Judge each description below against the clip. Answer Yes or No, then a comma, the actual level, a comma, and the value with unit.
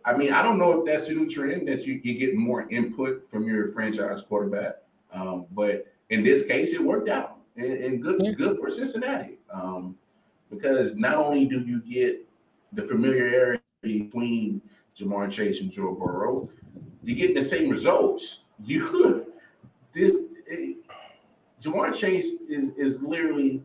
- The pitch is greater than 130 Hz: Yes, medium, 140 Hz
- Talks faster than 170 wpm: No, average, 160 wpm